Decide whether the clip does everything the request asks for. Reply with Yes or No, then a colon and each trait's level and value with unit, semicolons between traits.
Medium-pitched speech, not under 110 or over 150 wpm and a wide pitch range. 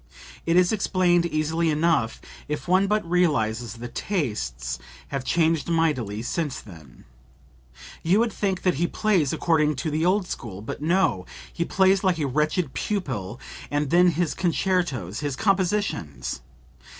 Yes: medium, 160 Hz; average, 140 wpm; wide, 6.0 semitones